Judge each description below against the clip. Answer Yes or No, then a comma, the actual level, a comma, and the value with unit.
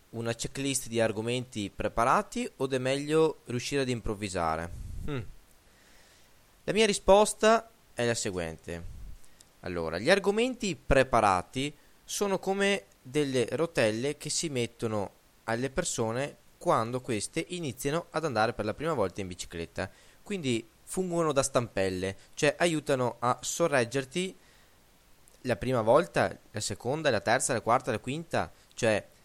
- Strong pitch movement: Yes, wide, 7.5 semitones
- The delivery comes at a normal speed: Yes, average, 125 wpm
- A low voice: Yes, low, 125 Hz